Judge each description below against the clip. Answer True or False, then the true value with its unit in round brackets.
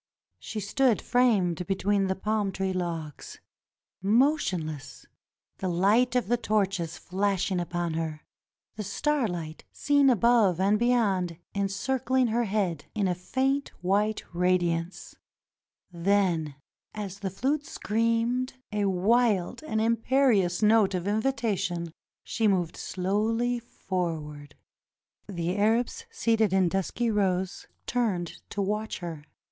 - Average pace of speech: False (120 wpm)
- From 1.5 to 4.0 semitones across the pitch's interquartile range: False (4.4 semitones)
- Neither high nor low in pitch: False (200 Hz)